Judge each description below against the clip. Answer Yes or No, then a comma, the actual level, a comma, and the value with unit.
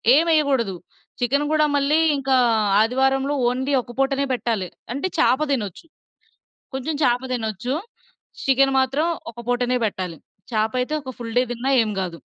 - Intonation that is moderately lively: Yes, average, 3.1 semitones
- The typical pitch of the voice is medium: No, very high, 255 Hz